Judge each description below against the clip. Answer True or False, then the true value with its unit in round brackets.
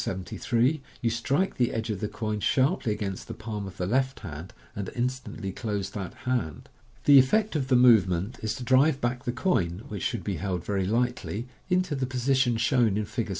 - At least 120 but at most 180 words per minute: False (195 wpm)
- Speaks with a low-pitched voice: True (115 Hz)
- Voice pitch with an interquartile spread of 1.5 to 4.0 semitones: False (4.4 semitones)